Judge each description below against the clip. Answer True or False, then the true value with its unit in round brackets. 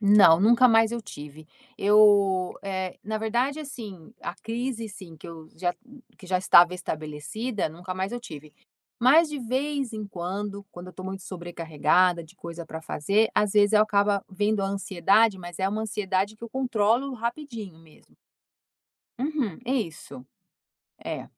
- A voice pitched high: True (200 Hz)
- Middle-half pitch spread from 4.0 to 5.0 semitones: True (4.3 semitones)